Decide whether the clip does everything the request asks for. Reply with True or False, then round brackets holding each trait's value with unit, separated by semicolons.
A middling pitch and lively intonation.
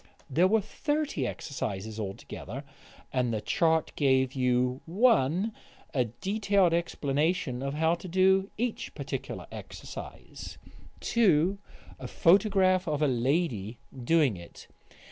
True (160 Hz; 6.9 semitones)